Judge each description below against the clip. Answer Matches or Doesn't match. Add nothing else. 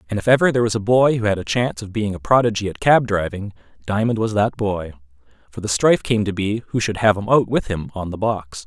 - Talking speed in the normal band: Doesn't match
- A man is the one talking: Matches